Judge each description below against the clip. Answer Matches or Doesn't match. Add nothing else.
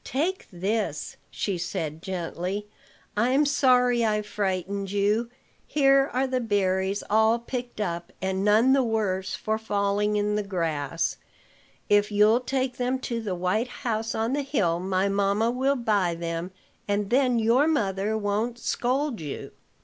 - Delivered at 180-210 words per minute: Doesn't match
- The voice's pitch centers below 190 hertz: Doesn't match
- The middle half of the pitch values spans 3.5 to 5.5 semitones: Matches